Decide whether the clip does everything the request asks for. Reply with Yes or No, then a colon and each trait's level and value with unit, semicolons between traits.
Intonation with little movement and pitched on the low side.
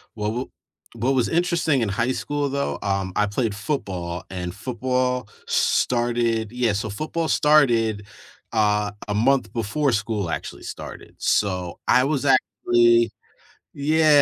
No: average, 4.6 semitones; low, 115 Hz